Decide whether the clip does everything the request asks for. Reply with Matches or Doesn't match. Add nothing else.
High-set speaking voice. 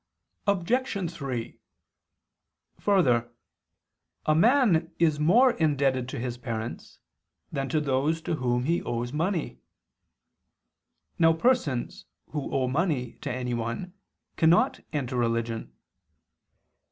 Doesn't match